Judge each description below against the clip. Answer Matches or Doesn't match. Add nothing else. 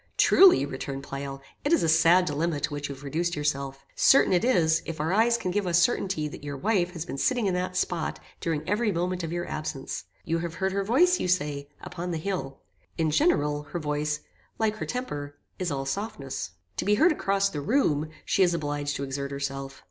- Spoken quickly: Matches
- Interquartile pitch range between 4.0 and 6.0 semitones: Matches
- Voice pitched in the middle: Matches